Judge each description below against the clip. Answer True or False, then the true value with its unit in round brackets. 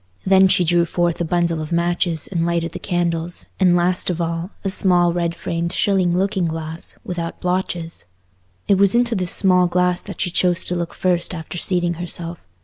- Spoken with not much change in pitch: True (1.4 semitones)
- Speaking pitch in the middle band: True (175 Hz)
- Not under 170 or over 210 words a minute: True (190 wpm)